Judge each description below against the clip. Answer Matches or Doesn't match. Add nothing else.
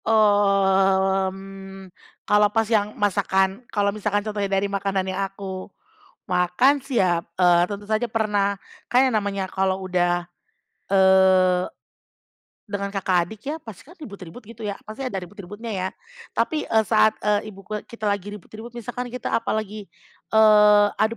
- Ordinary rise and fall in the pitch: Doesn't match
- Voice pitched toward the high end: Matches